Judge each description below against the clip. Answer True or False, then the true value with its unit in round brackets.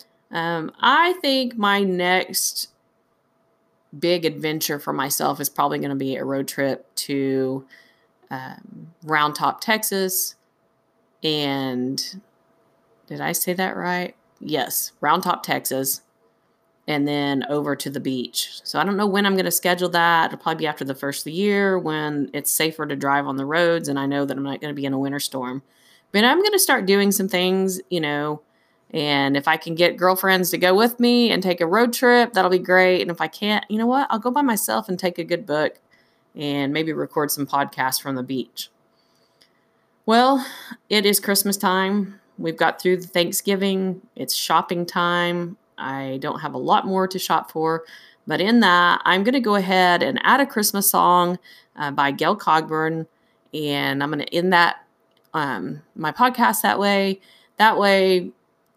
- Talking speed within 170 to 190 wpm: True (185 wpm)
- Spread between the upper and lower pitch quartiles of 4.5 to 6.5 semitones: True (5.1 semitones)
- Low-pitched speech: False (175 Hz)